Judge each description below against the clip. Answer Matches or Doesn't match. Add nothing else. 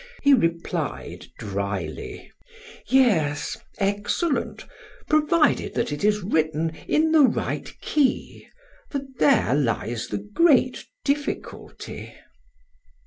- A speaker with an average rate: Doesn't match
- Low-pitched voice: Doesn't match